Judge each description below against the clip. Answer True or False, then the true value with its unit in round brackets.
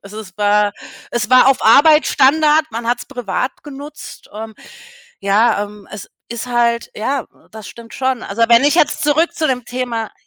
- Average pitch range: True (4.1 semitones)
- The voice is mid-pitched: False (240 Hz)